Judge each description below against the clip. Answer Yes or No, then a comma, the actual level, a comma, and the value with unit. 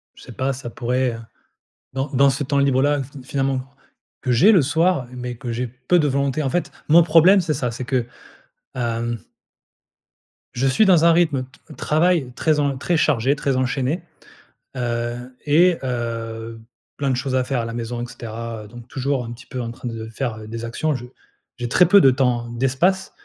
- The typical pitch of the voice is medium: No, low, 130 Hz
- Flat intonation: No, average, 3.4 semitones